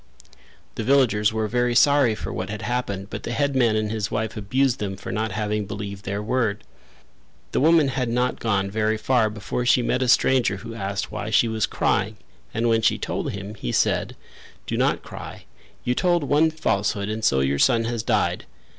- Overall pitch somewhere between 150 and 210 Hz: No, low, 110 Hz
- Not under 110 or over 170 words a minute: No, average, 195 wpm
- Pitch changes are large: No, average, 3.2 semitones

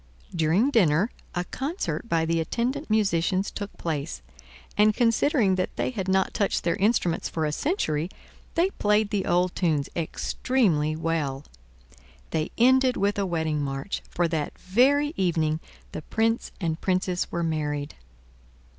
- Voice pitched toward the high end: No, medium, 180 Hz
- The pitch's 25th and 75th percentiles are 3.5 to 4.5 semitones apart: No, wide, 5.6 semitones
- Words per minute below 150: Yes, average, 140 wpm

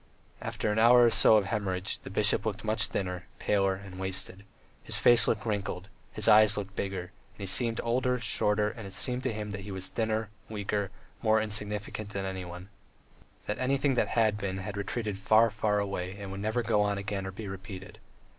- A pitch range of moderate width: No, narrow, 2.1 semitones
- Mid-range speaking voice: No, low, 105 Hz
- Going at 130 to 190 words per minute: No, average, 200 wpm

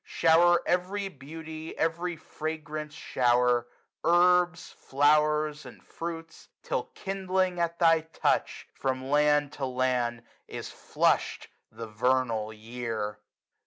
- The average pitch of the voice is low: No, medium, 150 Hz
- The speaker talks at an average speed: No, slow, 105 wpm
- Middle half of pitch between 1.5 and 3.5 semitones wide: No, average, 4.9 semitones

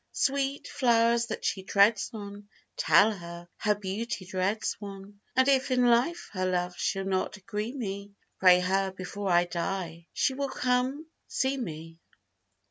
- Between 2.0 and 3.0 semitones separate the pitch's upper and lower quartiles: No, average, 4.3 semitones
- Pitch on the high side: Yes, high, 200 Hz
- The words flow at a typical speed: Yes, average, 150 wpm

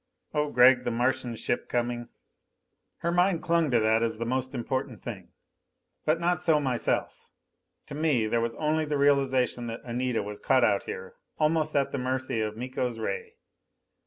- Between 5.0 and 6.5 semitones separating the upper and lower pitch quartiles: No, average, 4.3 semitones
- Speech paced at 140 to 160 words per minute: No, average, 170 wpm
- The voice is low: Yes, low, 130 Hz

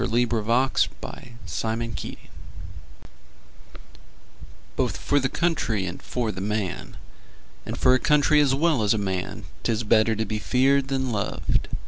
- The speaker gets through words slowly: Yes, slow, 130 wpm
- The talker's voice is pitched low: Yes, low, 115 Hz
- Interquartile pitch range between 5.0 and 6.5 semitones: No, average, 4.1 semitones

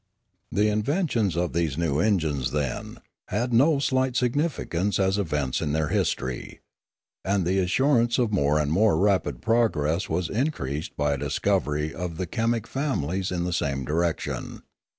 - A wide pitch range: Yes, wide, 7.3 semitones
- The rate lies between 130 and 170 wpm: Yes, average, 155 wpm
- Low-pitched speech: Yes, very low, 90 Hz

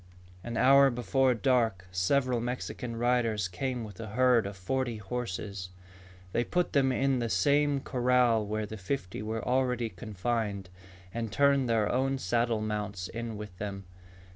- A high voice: No, low, 115 Hz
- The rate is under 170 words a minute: Yes, average, 150 wpm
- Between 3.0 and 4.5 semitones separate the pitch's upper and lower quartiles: Yes, average, 3.3 semitones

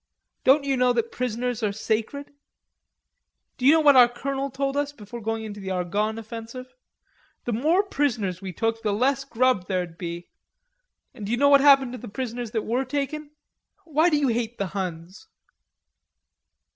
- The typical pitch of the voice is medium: No, high, 240 Hz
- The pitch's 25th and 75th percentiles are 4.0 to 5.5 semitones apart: Yes, average, 4.4 semitones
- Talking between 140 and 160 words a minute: No, average, 170 wpm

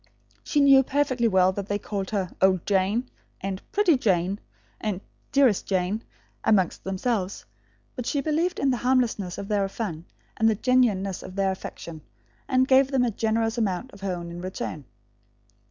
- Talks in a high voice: Yes, high, 205 Hz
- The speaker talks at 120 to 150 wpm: No, average, 170 wpm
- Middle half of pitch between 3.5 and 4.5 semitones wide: No, average, 5.1 semitones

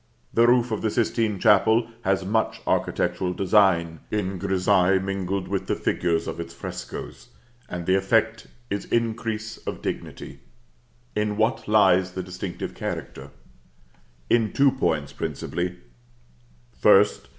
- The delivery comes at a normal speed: No, slow, 130 wpm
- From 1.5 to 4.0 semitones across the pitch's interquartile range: Yes, average, 3.4 semitones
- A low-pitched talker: Yes, low, 100 Hz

